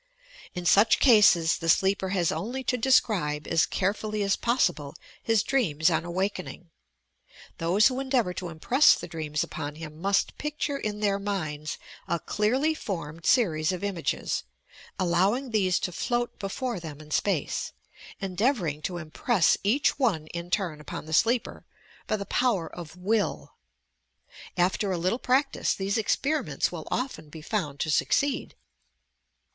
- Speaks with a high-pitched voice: Yes, high, 195 Hz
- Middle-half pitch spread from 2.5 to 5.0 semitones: No, wide, 5.6 semitones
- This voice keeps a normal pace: Yes, average, 150 wpm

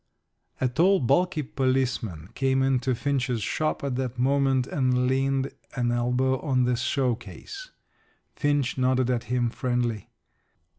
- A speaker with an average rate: No, slow, 130 wpm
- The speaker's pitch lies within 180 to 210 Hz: No, low, 130 Hz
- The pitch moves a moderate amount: No, narrow, 1.7 semitones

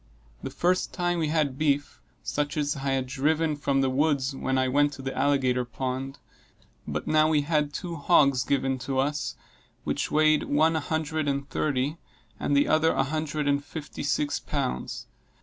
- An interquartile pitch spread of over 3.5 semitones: No, narrow, 2.4 semitones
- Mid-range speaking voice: Yes, medium, 145 Hz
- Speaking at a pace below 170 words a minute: No, average, 180 wpm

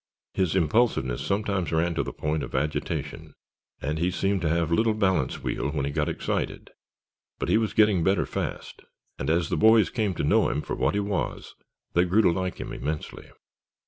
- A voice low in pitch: Yes, very low, 90 Hz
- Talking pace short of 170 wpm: No, average, 195 wpm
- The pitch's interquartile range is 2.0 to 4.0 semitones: No, average, 4.5 semitones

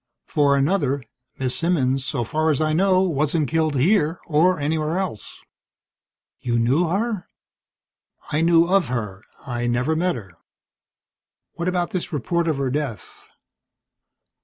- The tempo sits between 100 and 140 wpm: Yes, slow, 135 wpm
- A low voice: No, medium, 155 Hz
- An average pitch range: Yes, average, 4.6 semitones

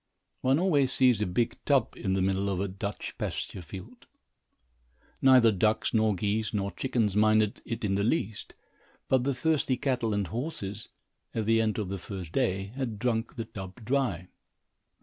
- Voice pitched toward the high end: No, low, 110 Hz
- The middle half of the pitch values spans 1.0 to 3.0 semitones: No, average, 4.2 semitones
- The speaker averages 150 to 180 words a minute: Yes, average, 170 wpm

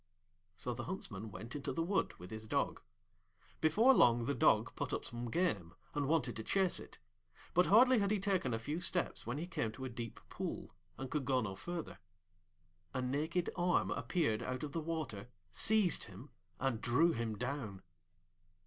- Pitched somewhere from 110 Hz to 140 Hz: Yes, low, 135 Hz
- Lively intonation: Yes, wide, 6.7 semitones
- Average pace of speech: Yes, average, 185 wpm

